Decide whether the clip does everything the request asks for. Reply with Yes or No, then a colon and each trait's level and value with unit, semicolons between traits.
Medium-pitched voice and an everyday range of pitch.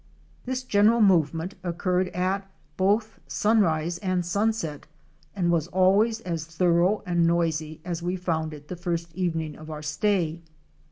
Yes: medium, 175 Hz; average, 3.1 semitones